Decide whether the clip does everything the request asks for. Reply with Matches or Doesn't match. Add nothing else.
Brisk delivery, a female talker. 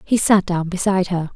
Matches